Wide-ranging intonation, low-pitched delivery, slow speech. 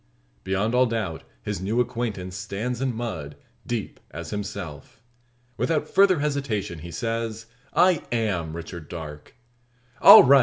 Yes: wide, 5.7 semitones; low, 110 Hz; slow, 130 wpm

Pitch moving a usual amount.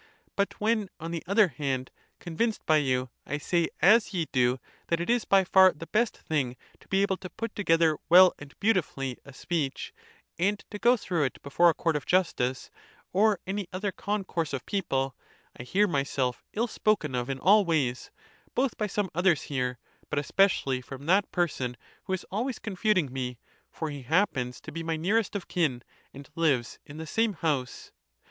No: wide, 6.3 semitones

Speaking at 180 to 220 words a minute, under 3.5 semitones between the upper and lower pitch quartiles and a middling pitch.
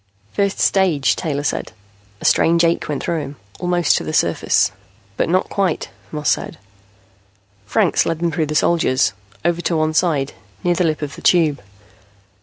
No: average, 170 wpm; narrow, 2.6 semitones; medium, 165 Hz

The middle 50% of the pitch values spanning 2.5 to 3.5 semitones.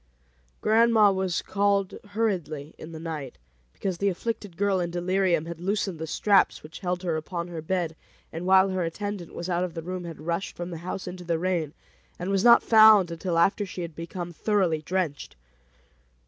Yes: average, 2.8 semitones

